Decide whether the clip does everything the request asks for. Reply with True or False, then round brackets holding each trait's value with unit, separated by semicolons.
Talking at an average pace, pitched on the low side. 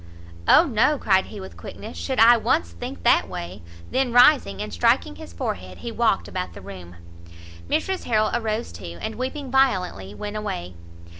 False (175 wpm; 190 Hz)